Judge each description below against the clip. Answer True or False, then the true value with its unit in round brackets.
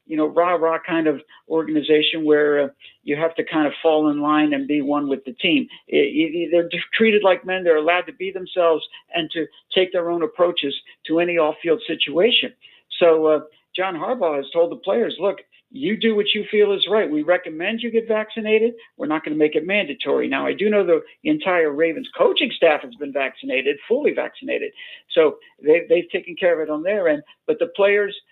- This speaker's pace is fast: True (210 wpm)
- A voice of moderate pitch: True (175 Hz)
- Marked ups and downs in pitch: True (6.1 semitones)